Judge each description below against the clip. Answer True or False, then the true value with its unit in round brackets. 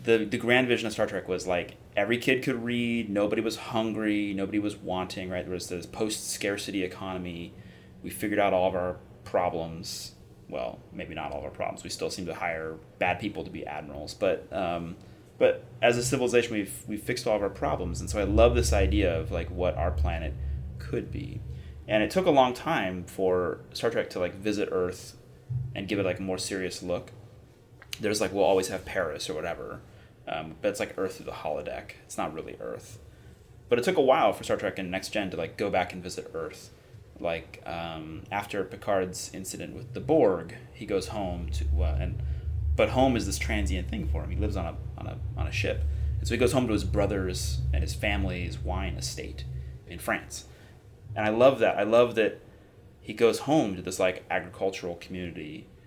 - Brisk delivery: True (210 wpm)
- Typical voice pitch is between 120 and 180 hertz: False (95 Hz)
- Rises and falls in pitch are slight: False (4.1 semitones)